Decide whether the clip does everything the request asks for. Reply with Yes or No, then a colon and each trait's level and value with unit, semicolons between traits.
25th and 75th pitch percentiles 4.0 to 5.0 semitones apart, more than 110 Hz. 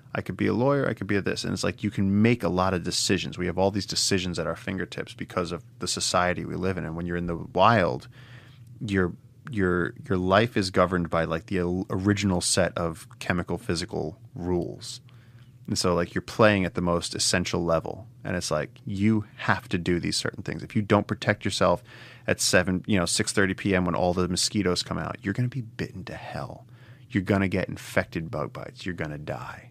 No: average, 4.5 semitones; very low, 95 Hz